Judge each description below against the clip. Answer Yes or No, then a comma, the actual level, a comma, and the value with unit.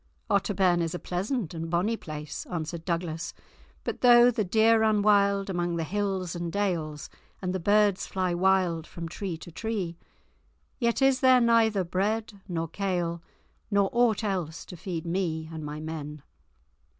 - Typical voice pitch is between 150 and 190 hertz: Yes, medium, 185 Hz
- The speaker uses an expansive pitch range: No, average, 3.7 semitones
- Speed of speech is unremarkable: Yes, average, 160 wpm